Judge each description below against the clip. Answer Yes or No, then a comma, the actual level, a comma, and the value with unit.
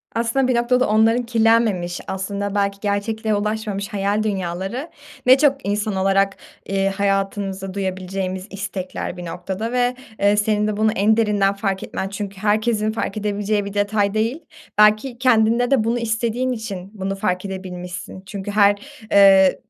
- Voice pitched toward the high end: Yes, high, 205 Hz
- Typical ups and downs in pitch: No, narrow, 2.2 semitones